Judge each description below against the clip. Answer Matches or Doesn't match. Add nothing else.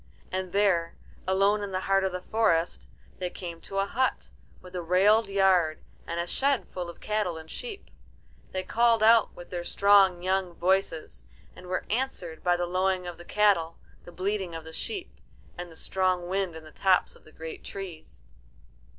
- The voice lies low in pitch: Doesn't match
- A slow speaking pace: Doesn't match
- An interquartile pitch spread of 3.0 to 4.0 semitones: Doesn't match